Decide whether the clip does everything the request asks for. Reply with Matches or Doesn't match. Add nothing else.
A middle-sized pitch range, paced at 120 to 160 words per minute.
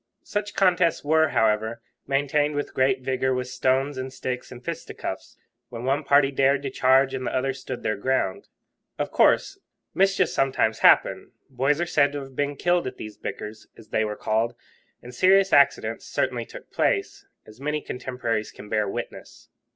Doesn't match